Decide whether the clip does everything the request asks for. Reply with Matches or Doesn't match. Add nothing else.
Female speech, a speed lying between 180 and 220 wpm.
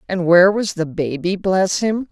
Matches